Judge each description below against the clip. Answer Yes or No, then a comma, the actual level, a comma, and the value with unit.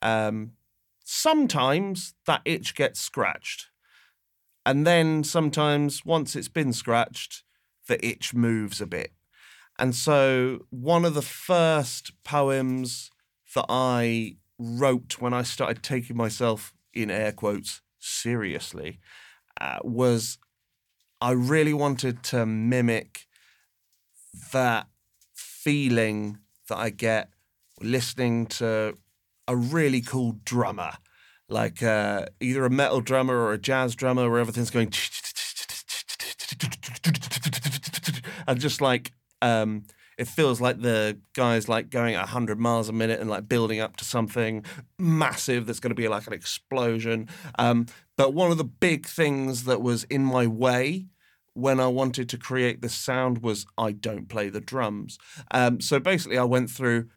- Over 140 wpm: No, slow, 135 wpm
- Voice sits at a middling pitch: No, low, 125 Hz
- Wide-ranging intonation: No, average, 3.0 semitones